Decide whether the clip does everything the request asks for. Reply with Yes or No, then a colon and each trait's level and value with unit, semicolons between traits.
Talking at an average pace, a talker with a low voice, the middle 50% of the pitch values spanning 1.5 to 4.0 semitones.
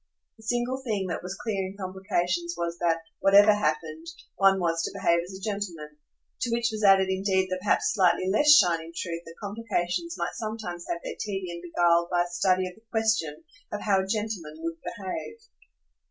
No: average, 185 wpm; high, 190 Hz; average, 3.5 semitones